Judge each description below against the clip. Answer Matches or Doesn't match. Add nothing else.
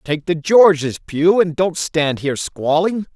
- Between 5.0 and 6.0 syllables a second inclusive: Doesn't match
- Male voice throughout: Matches